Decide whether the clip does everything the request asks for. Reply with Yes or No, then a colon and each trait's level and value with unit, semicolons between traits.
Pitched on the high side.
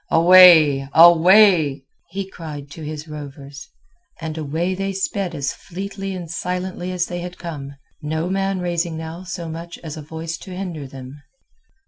No: medium, 170 Hz